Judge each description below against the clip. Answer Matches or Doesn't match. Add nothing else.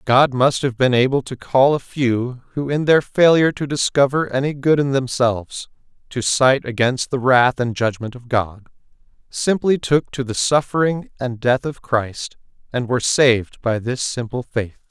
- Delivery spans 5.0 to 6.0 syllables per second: Doesn't match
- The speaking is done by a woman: Doesn't match